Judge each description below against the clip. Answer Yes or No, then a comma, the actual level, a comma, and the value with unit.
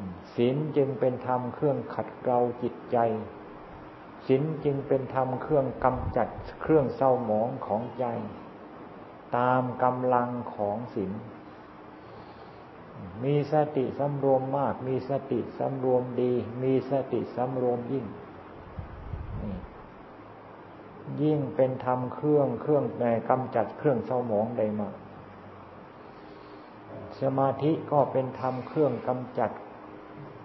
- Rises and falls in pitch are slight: No, average, 3.4 semitones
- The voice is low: Yes, low, 125 Hz